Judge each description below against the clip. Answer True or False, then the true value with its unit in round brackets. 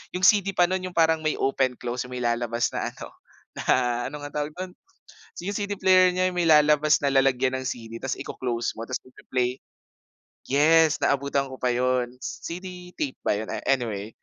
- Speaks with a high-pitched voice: False (140 Hz)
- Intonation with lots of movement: True (5.8 semitones)